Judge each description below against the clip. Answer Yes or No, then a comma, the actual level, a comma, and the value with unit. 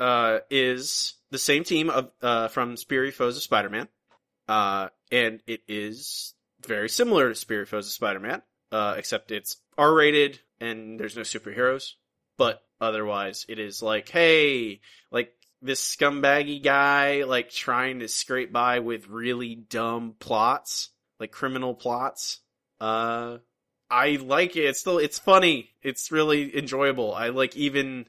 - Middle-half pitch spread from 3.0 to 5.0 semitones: Yes, average, 3.7 semitones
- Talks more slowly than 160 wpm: Yes, average, 150 wpm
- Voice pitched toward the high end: No, low, 125 Hz